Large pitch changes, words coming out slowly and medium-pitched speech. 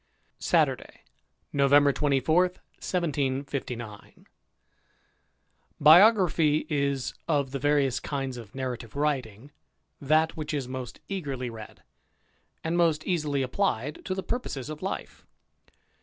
No: average, 3.3 semitones; slow, 110 wpm; medium, 145 Hz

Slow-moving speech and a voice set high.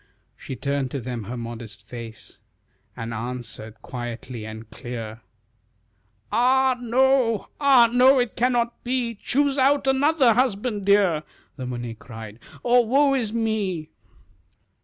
Yes: slow, 125 wpm; high, 205 Hz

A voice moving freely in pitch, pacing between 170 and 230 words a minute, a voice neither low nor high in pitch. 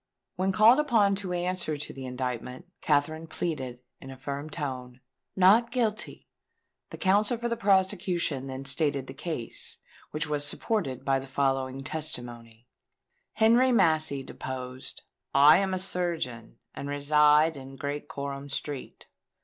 No: wide, 5.7 semitones; average, 140 wpm; medium, 150 Hz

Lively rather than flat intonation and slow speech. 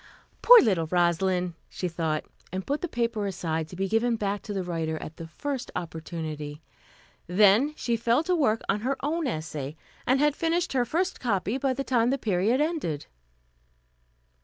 No: wide, 7.8 semitones; average, 175 wpm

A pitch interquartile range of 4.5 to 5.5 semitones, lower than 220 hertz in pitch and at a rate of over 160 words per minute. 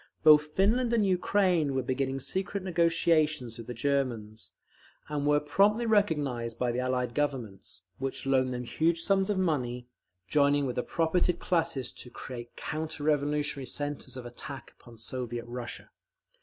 No: average, 4.9 semitones; medium, 140 Hz; average, 150 wpm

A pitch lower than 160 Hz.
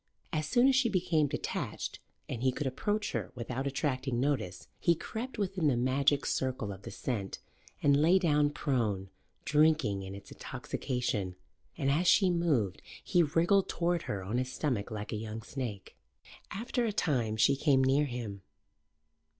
Yes: low, 135 Hz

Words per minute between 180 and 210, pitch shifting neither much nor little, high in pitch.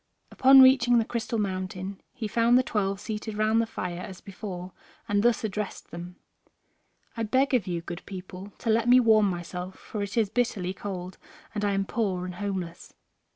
Yes: average, 185 wpm; average, 3.6 semitones; high, 205 Hz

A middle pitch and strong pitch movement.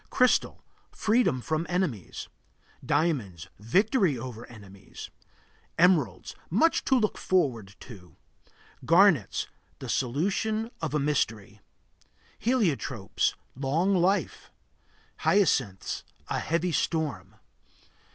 Yes: medium, 155 Hz; wide, 8.5 semitones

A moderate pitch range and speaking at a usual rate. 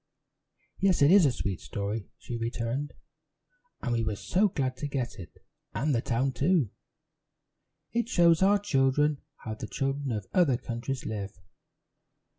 Yes: average, 4.8 semitones; average, 150 wpm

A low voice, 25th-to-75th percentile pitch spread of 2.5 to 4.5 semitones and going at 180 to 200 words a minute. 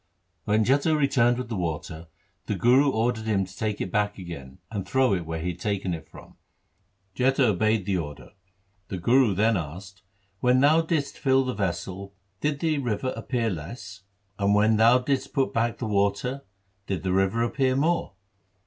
No: low, 110 Hz; average, 5.1 semitones; average, 185 wpm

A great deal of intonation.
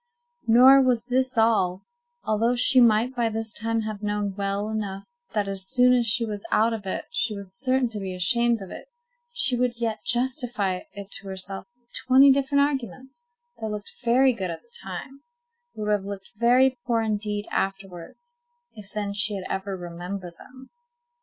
No: average, 3.9 semitones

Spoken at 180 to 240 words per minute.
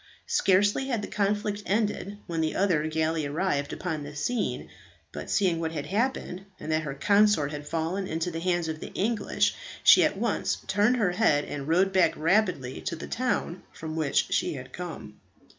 Yes: average, 185 wpm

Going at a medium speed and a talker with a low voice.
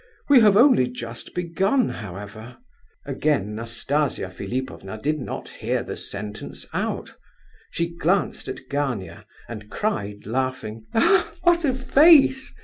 No: slow, 120 wpm; low, 130 Hz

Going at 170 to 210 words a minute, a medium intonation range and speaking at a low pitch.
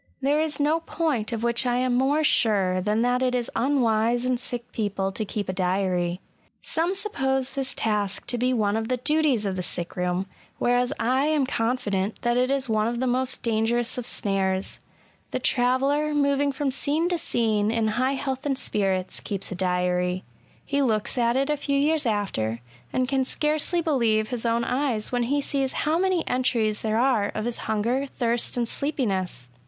No: average, 190 wpm; average, 4.3 semitones; high, 245 Hz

